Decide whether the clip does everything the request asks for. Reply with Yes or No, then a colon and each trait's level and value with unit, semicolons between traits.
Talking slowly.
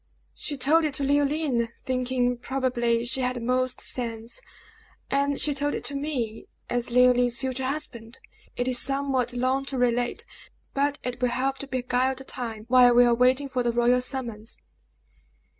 No: average, 170 wpm